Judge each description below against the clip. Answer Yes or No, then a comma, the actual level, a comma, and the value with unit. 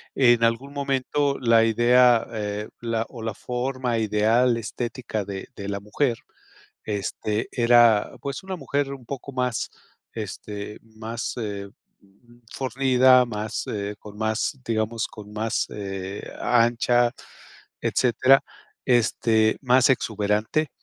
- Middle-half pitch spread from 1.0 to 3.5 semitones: Yes, average, 2.9 semitones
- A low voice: Yes, low, 115 Hz